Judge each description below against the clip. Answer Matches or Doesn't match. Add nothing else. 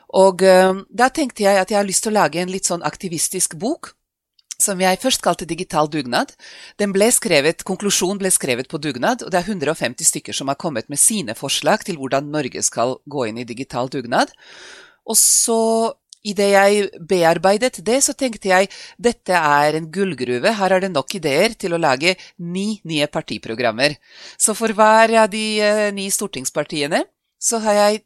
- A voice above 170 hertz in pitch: Matches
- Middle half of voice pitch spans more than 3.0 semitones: Matches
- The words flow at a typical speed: Matches